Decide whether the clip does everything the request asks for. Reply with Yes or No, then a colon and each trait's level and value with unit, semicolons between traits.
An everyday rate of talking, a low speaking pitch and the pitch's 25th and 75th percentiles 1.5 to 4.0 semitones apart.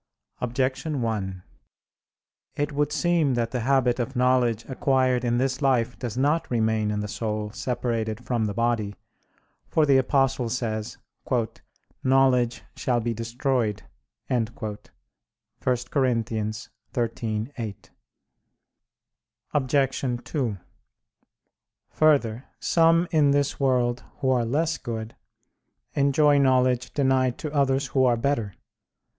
No: slow, 110 wpm; low, 125 Hz; average, 2.9 semitones